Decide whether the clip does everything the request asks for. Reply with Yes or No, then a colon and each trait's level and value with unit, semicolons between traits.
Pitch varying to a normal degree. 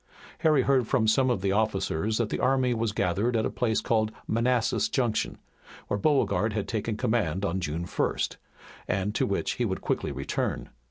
Yes: average, 3.7 semitones